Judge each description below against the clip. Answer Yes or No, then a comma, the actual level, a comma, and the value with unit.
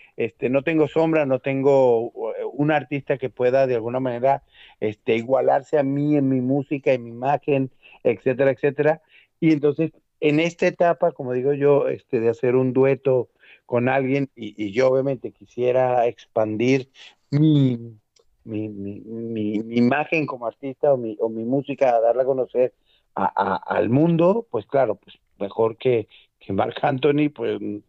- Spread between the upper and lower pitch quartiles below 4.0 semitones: Yes, average, 3.6 semitones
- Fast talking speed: No, average, 165 wpm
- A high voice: No, low, 135 Hz